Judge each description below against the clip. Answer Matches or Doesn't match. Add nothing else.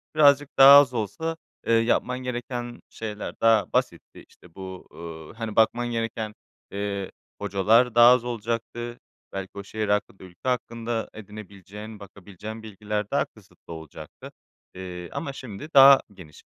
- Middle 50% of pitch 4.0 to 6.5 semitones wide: Doesn't match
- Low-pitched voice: Matches